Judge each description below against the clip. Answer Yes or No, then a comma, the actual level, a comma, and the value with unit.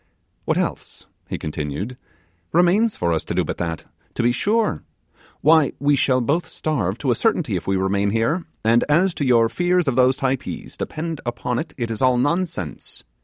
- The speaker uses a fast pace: No, average, 185 wpm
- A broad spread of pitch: Yes, wide, 6.6 semitones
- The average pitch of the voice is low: Yes, low, 130 Hz